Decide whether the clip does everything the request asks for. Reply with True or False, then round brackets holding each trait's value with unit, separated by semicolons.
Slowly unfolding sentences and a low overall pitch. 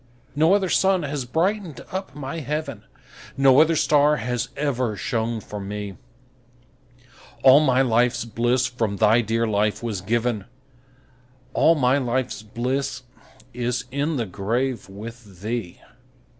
True (130 wpm; 125 Hz)